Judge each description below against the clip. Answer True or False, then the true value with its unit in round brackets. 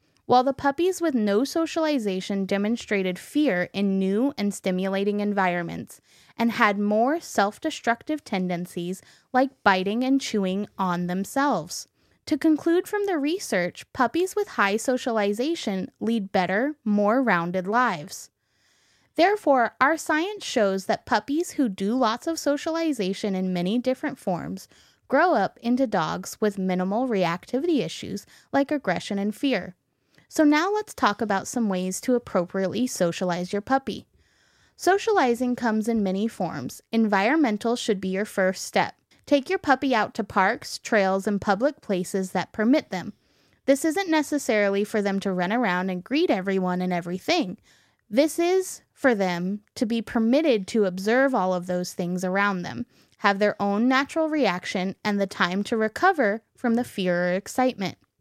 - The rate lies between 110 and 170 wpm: True (150 wpm)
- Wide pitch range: True (6.1 semitones)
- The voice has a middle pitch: False (215 Hz)